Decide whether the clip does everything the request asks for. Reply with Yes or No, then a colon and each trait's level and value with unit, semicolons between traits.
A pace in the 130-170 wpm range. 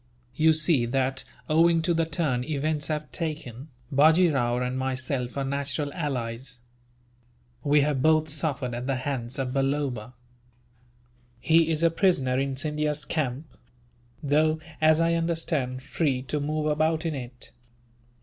Yes: average, 140 wpm